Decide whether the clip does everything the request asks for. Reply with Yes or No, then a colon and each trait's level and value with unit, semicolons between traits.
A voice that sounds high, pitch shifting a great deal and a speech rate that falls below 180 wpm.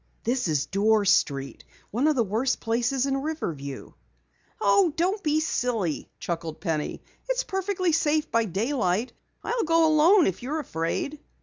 Yes: very high, 255 Hz; wide, 8.6 semitones; average, 145 wpm